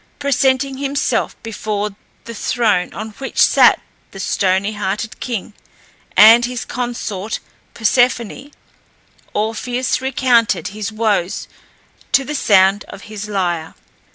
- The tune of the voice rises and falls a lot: No, average, 3.6 semitones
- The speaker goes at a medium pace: No, slow, 110 wpm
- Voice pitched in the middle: No, high, 220 Hz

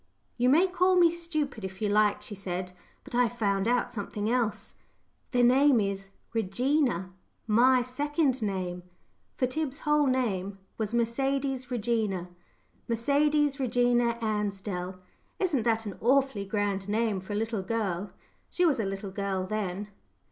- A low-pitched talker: No, high, 230 Hz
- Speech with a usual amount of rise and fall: Yes, average, 5.0 semitones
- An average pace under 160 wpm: Yes, average, 145 wpm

